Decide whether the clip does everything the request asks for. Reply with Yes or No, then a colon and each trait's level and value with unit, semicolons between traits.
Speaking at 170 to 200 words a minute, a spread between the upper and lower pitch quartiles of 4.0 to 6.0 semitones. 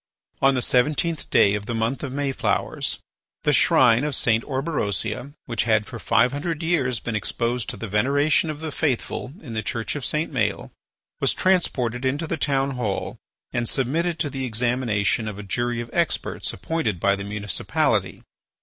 Yes: average, 175 wpm; average, 4.4 semitones